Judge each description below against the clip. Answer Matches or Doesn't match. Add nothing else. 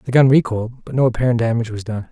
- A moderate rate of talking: Doesn't match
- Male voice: Matches